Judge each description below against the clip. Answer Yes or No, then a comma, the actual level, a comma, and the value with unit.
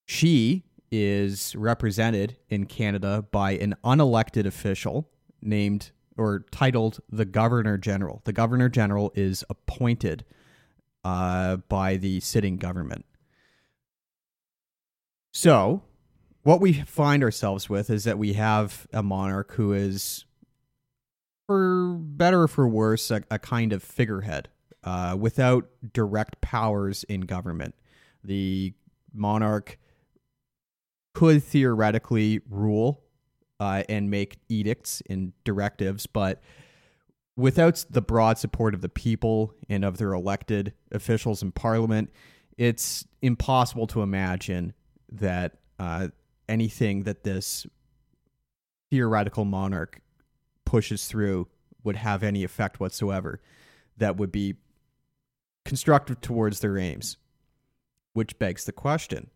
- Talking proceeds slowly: Yes, slow, 110 wpm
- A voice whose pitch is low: Yes, low, 110 Hz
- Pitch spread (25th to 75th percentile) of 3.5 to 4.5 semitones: Yes, average, 3.9 semitones